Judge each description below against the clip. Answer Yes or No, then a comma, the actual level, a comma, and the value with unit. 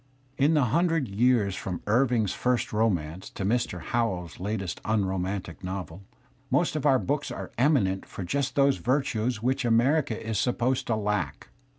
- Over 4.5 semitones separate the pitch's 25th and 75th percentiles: Yes, average, 5.3 semitones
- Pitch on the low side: Yes, low, 115 Hz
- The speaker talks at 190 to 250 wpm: No, average, 160 wpm